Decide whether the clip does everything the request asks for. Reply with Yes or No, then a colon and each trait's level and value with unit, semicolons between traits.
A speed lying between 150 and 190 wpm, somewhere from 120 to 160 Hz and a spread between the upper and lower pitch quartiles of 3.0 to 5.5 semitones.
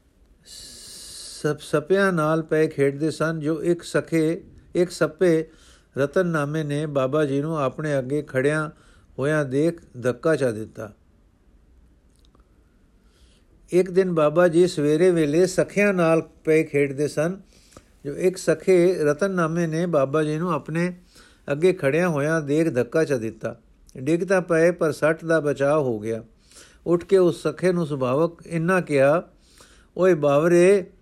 No: average, 135 wpm; medium, 155 Hz; average, 3.6 semitones